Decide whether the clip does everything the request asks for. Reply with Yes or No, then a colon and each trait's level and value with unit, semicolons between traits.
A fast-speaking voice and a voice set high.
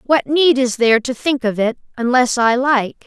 Yes: fast, 215 wpm; very high, 250 Hz